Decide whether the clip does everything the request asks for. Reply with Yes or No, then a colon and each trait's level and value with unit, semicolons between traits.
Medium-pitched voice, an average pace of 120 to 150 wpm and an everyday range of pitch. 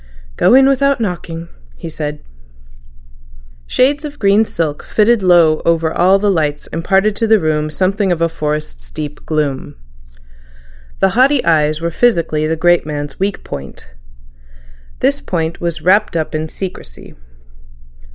Yes: medium, 170 Hz; average, 140 wpm; average, 4.8 semitones